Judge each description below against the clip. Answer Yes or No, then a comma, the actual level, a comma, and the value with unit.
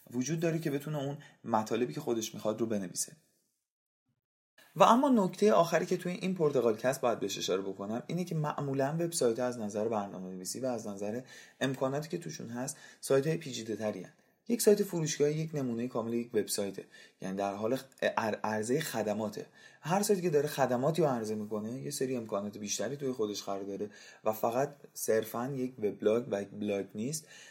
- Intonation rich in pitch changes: Yes, wide, 6.3 semitones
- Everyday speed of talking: No, fast, 170 wpm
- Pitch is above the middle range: No, low, 130 Hz